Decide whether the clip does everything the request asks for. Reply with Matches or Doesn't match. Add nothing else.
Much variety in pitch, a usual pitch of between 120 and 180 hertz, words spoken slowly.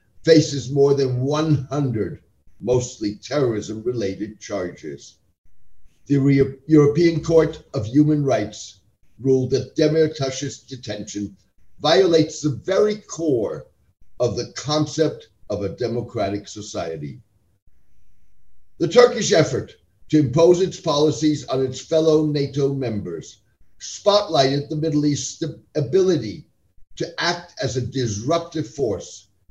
Matches